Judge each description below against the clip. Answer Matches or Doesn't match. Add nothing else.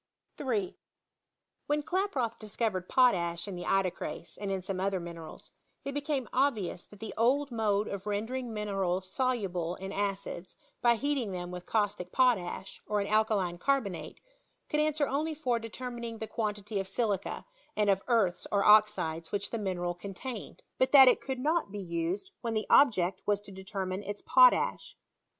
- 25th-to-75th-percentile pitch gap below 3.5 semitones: Doesn't match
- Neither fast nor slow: Matches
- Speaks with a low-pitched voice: Doesn't match